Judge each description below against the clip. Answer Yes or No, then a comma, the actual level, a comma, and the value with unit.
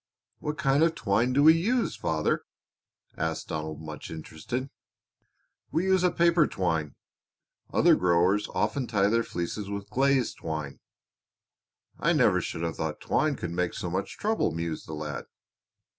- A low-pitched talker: Yes, low, 100 Hz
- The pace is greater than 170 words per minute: No, average, 150 wpm